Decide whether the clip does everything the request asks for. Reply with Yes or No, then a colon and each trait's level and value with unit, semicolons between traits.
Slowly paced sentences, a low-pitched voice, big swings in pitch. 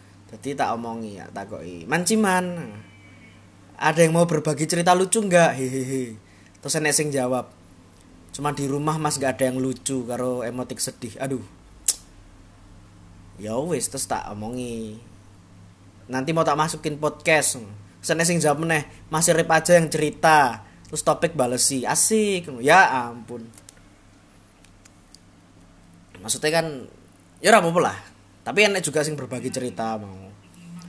No: average, 130 wpm; low, 125 Hz; wide, 7.7 semitones